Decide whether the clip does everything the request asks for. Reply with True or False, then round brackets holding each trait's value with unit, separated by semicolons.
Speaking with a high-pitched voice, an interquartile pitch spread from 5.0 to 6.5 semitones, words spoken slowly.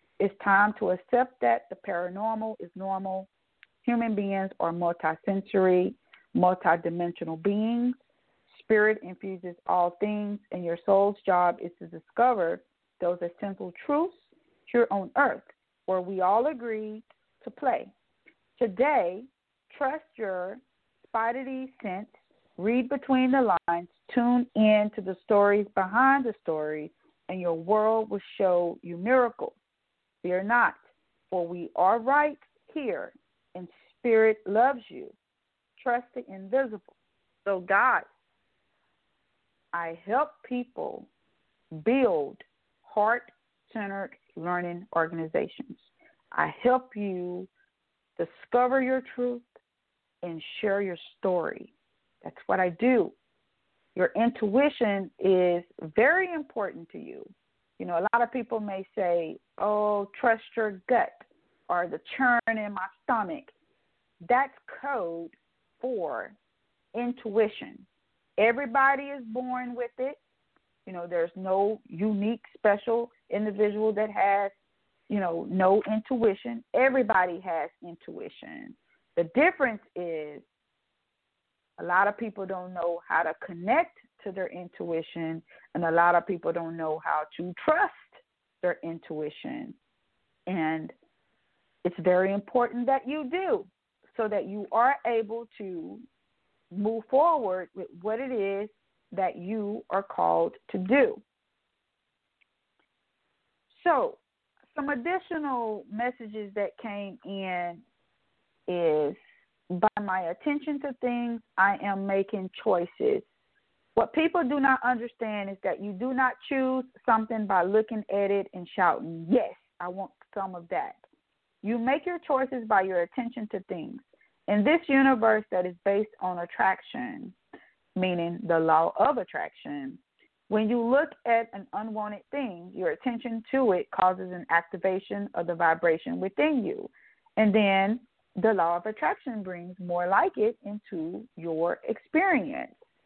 True (210 Hz; 5.4 semitones; 125 wpm)